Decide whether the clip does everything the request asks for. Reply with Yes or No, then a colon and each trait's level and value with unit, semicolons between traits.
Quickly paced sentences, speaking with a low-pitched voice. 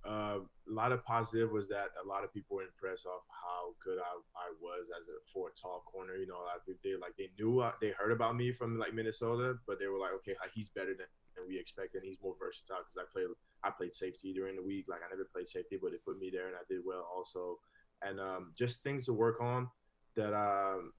Yes: fast, 260 wpm; low, 115 Hz